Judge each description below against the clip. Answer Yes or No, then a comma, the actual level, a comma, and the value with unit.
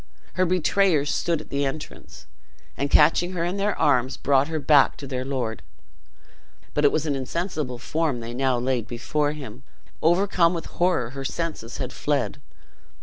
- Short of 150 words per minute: No, average, 165 wpm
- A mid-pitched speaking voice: Yes, medium, 145 Hz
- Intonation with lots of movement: No, average, 4.2 semitones